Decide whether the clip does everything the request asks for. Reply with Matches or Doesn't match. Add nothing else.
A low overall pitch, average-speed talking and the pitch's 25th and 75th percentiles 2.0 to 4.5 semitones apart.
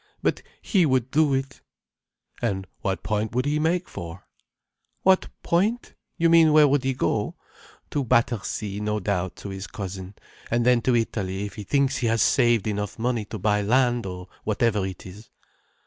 Doesn't match